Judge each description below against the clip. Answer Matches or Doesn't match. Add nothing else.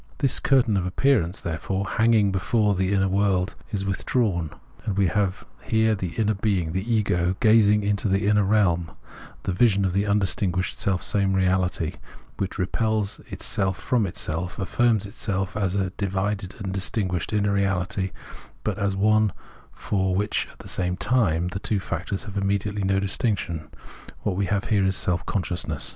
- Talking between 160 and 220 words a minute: Matches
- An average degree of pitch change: Doesn't match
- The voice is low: Matches